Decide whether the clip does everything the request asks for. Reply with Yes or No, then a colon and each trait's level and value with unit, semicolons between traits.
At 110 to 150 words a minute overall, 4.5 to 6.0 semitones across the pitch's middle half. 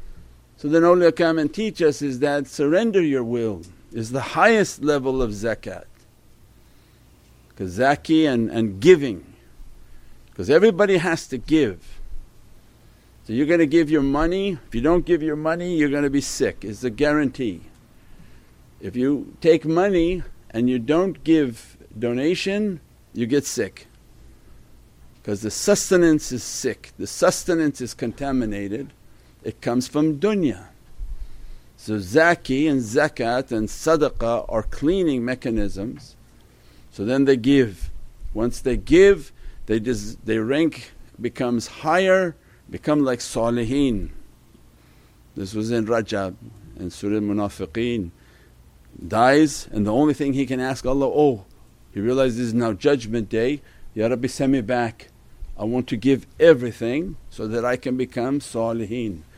Yes: average, 140 wpm; average, 5.1 semitones